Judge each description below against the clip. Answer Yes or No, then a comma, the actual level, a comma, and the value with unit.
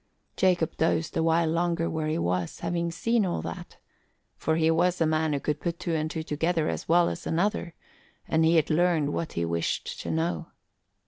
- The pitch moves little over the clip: Yes, narrow, 1.8 semitones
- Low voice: No, medium, 160 Hz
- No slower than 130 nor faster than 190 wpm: No, average, 200 wpm